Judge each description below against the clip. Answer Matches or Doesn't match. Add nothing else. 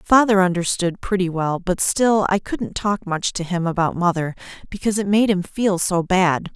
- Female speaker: Matches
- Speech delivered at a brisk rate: Doesn't match